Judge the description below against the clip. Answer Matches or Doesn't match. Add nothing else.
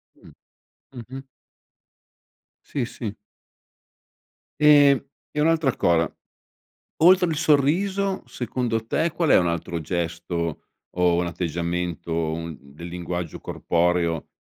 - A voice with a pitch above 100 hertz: Doesn't match